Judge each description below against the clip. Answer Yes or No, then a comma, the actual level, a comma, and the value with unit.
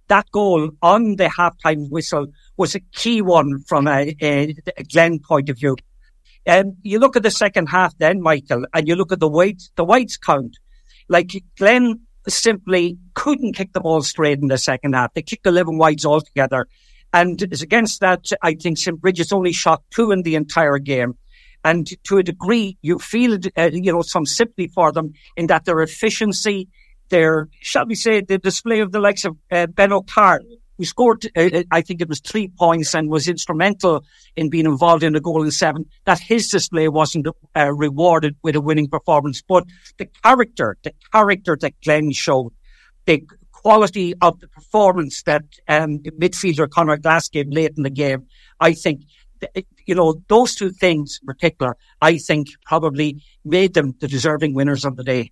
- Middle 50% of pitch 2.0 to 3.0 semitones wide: No, average, 3.8 semitones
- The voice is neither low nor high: Yes, medium, 170 Hz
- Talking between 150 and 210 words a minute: Yes, average, 190 wpm